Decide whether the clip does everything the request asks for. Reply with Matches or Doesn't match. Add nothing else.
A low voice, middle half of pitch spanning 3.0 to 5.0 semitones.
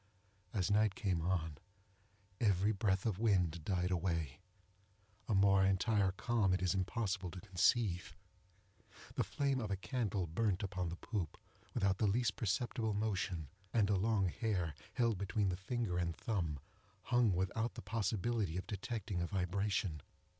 Matches